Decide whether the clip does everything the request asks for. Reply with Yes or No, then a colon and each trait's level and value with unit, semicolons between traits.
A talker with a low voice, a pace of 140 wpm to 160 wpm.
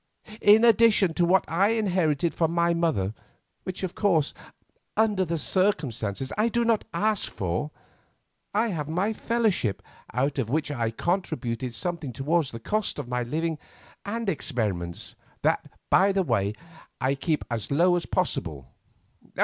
No: medium, 165 Hz; average, 150 wpm